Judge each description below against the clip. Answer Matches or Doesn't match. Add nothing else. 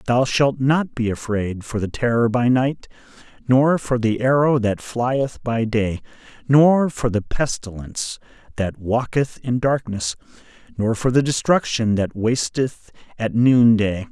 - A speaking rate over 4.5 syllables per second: Doesn't match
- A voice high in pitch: Doesn't match